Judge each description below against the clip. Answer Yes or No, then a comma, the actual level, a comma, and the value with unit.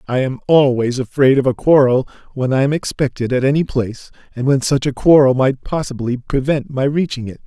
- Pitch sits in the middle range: No, low, 130 Hz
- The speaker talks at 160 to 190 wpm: No, average, 200 wpm